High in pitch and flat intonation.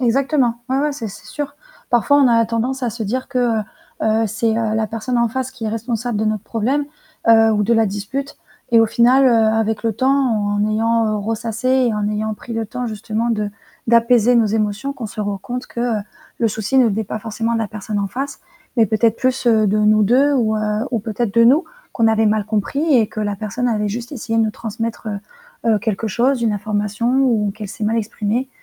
Yes: high, 225 Hz; narrow, 2.3 semitones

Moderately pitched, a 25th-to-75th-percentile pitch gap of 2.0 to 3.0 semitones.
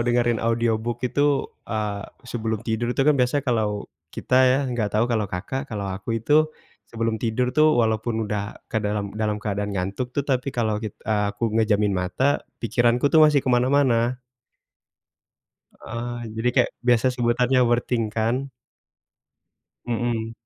No: low, 115 Hz; narrow, 2.6 semitones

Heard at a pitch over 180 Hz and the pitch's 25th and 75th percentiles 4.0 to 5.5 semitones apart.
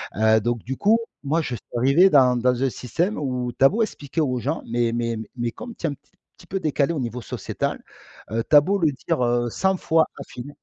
No: low, 135 Hz; average, 5.1 semitones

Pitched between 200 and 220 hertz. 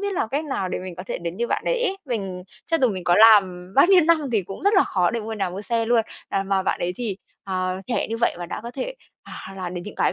Yes: high, 210 Hz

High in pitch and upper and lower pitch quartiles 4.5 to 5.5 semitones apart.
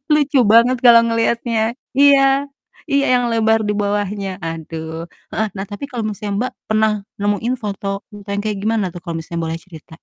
No: high, 215 Hz; average, 3.1 semitones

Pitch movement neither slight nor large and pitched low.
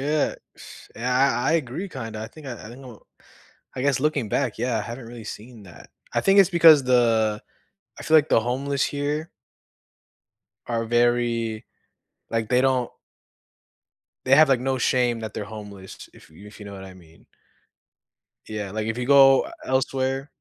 Yes: average, 3.6 semitones; low, 120 Hz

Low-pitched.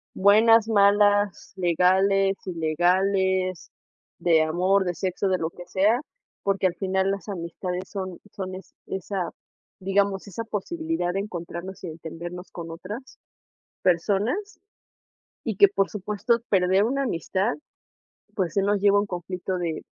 No: high, 190 Hz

